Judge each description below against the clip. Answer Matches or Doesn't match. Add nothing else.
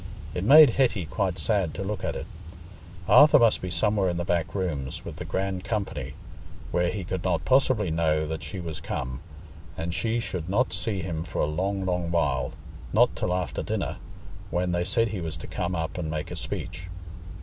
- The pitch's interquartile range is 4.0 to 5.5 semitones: Doesn't match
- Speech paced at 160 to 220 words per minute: Matches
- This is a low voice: Matches